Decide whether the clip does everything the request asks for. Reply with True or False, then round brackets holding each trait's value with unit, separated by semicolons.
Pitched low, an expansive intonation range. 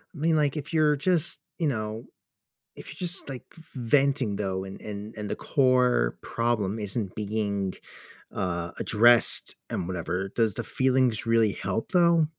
True (115 Hz; 5.8 semitones)